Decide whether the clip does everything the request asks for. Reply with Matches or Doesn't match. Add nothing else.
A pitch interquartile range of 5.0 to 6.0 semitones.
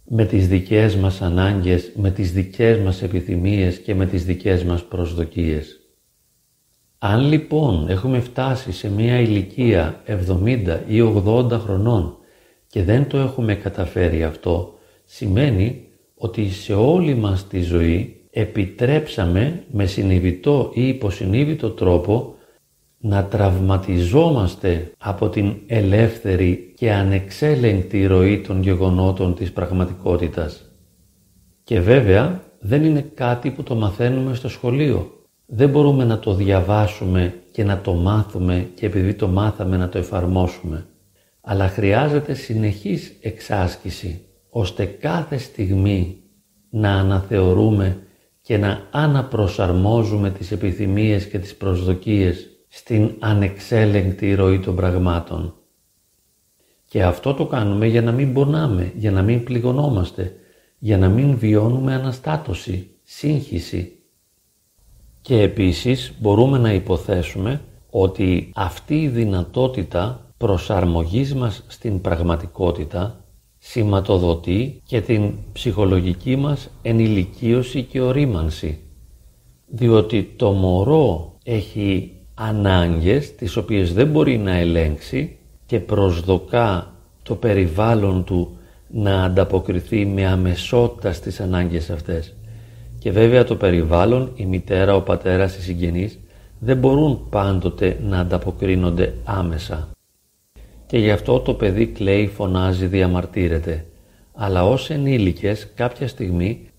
Doesn't match